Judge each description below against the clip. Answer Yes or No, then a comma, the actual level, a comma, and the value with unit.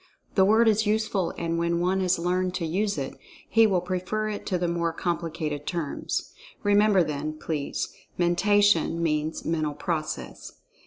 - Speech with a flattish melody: No, average, 3.8 semitones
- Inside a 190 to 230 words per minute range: No, average, 150 wpm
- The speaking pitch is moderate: Yes, medium, 175 Hz